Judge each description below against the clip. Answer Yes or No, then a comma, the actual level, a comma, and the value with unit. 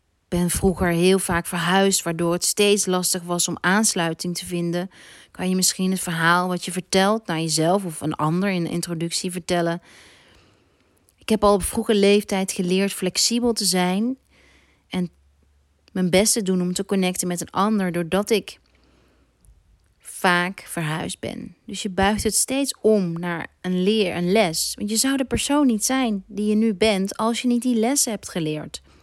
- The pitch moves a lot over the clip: No, average, 3.4 semitones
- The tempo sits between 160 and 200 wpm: Yes, average, 180 wpm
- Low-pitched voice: No, medium, 185 Hz